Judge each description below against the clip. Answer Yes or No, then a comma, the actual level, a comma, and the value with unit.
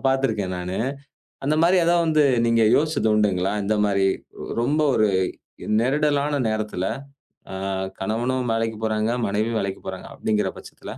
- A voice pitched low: Yes, low, 110 Hz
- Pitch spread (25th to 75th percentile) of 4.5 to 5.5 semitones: Yes, average, 5.2 semitones